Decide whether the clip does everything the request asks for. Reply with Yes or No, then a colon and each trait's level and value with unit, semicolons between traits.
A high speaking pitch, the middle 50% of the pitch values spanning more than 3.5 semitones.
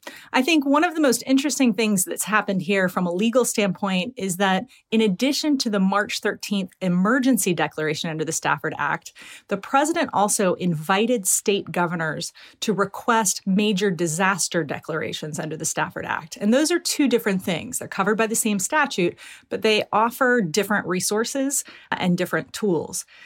Yes: high, 205 Hz; average, 5.1 semitones